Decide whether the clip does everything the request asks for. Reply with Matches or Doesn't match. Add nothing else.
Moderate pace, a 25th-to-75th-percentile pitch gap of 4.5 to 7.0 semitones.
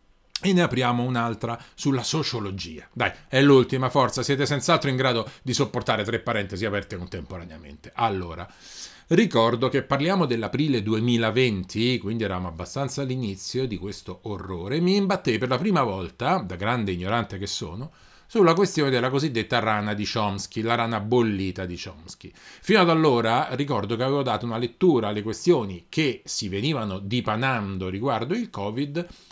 Matches